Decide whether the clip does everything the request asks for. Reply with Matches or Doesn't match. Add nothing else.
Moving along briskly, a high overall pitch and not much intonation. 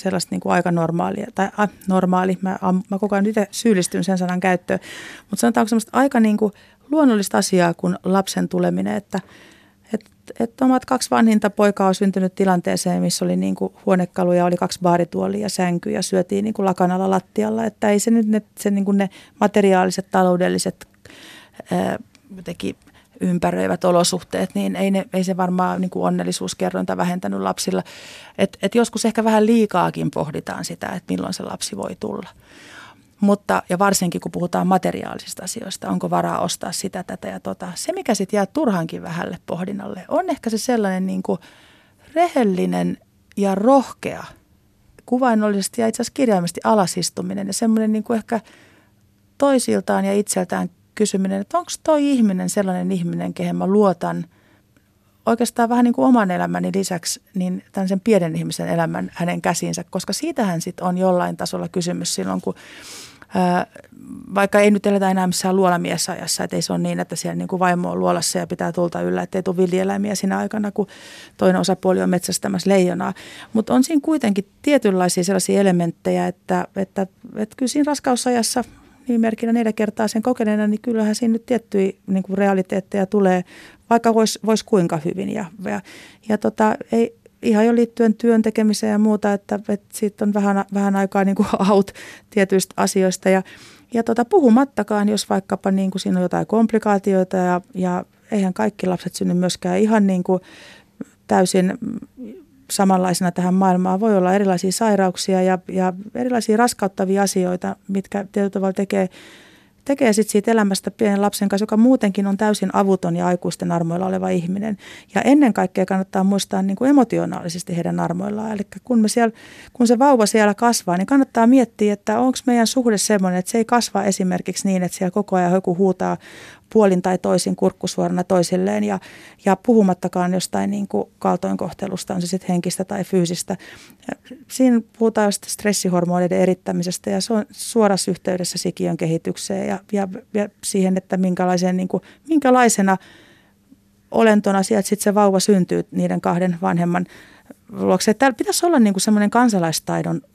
Doesn't match